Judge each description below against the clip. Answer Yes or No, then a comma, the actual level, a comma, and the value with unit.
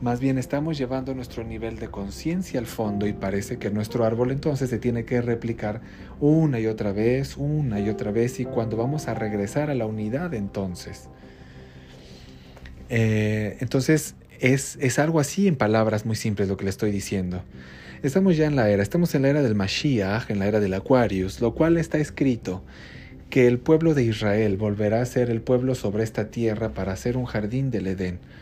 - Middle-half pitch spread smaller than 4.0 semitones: No, average, 4.5 semitones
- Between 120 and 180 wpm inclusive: No, fast, 190 wpm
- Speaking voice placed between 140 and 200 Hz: No, low, 115 Hz